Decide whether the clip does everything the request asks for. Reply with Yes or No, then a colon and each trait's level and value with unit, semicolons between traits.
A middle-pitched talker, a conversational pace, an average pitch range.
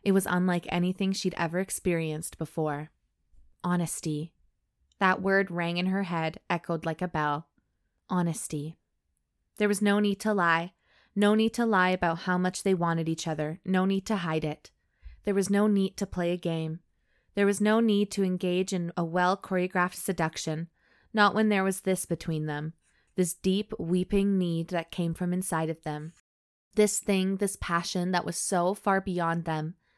Yes: medium, 180 Hz; average, 175 wpm; average, 3.2 semitones